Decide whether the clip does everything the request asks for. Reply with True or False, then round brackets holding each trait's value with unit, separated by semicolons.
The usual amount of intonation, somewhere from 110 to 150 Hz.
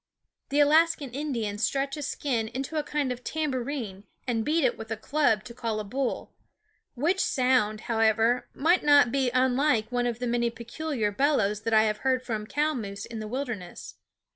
False (4.3 semitones; 250 Hz)